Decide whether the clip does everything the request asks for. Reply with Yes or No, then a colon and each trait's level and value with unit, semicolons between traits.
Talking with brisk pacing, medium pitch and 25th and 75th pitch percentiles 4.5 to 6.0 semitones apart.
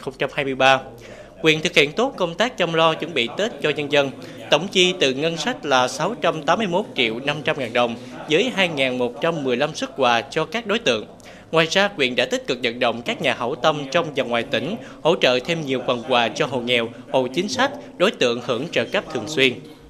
No: average, 210 wpm; medium, 150 Hz; average, 4.8 semitones